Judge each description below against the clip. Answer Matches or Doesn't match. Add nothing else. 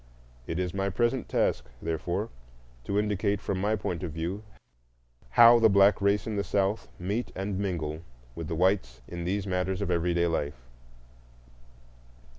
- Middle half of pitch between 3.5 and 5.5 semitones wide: Doesn't match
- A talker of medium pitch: Doesn't match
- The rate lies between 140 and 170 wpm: Matches